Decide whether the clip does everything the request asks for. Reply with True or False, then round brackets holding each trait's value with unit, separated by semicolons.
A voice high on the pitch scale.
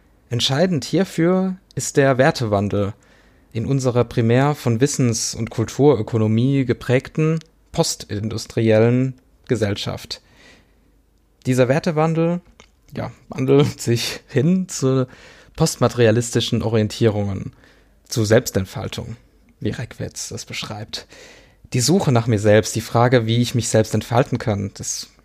False (120 Hz)